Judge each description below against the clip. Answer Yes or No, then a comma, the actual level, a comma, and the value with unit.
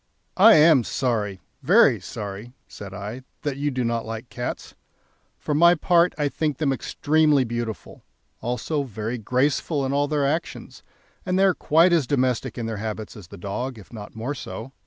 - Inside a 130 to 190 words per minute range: Yes, average, 180 wpm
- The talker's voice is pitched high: No, low, 130 Hz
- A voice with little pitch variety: No, average, 5.1 semitones